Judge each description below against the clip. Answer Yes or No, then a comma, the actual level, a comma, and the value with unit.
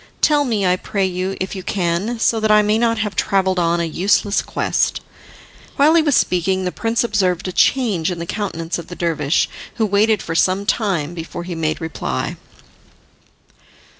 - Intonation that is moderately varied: Yes, average, 3.8 semitones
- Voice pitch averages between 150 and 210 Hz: Yes, high, 190 Hz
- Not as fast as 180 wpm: No, average, 185 wpm